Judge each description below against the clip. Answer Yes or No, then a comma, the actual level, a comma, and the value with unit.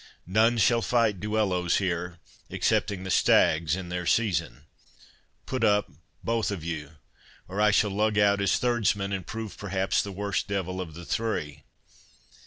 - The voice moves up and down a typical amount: Yes, average, 3.1 semitones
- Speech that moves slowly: No, average, 155 wpm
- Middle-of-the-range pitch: No, low, 100 Hz